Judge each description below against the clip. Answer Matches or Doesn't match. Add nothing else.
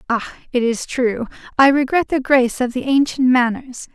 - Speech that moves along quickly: Doesn't match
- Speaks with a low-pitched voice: Doesn't match